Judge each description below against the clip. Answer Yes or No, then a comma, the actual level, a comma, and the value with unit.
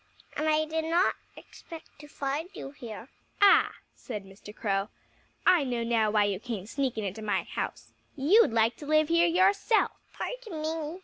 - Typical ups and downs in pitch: No, wide, 6.8 semitones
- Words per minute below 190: Yes, average, 170 wpm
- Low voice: No, very high, 290 Hz